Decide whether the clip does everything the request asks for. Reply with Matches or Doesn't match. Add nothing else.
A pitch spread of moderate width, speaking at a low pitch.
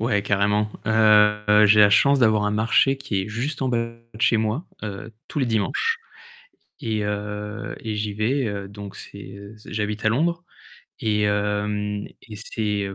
Doesn't match